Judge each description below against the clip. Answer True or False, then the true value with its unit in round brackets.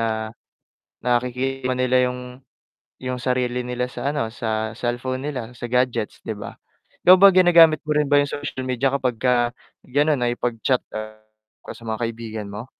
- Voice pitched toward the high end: False (125 Hz)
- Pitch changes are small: True (2.1 semitones)